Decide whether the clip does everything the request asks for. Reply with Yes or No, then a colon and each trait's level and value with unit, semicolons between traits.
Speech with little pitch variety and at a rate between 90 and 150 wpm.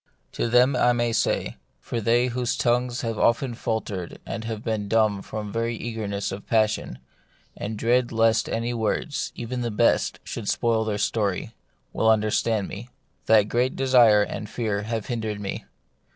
No: narrow, 2.0 semitones; average, 165 wpm